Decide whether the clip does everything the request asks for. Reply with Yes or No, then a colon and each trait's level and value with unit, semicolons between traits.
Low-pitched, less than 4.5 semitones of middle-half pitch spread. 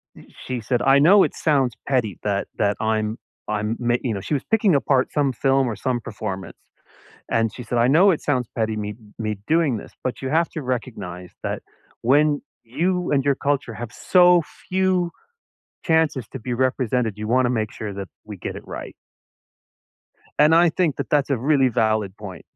No: low, 125 Hz; average, 5.3 semitones